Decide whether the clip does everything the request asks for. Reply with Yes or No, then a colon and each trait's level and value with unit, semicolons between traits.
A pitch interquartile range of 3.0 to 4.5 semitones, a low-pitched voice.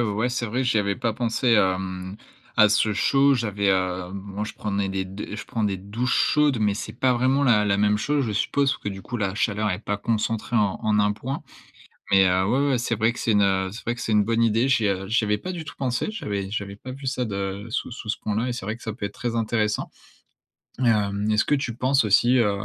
Yes: average, 3.3 semitones; low, 110 Hz